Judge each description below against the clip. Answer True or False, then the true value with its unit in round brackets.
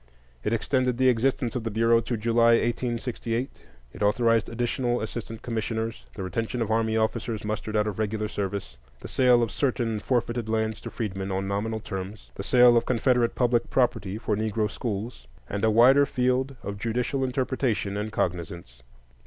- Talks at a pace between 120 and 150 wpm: False (170 wpm)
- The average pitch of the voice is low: True (115 Hz)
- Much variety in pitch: False (2.4 semitones)